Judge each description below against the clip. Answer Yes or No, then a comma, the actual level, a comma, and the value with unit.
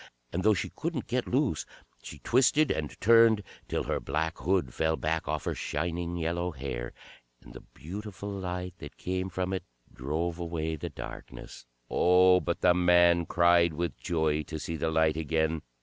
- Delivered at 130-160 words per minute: No, average, 170 wpm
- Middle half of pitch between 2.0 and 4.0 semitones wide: Yes, narrow, 2.6 semitones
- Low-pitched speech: Yes, very low, 85 Hz